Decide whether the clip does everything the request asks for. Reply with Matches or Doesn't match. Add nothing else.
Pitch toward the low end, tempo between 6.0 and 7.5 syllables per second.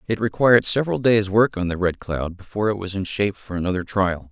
Matches